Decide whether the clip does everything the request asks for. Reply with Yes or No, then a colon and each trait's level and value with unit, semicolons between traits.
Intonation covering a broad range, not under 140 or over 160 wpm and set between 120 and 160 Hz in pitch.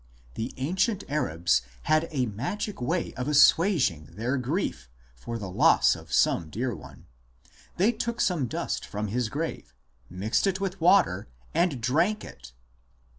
Yes: wide, 8.9 semitones; average, 145 wpm; low, 135 Hz